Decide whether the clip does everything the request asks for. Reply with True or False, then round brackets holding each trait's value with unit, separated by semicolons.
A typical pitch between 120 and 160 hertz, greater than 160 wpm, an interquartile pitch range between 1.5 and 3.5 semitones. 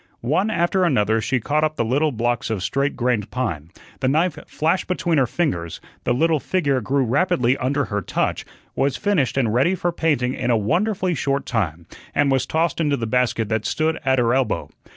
False (135 Hz; 195 wpm; 5.3 semitones)